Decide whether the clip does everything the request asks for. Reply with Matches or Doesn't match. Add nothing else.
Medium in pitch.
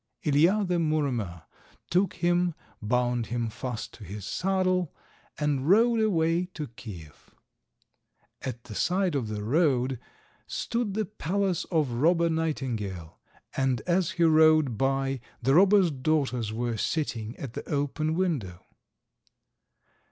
Matches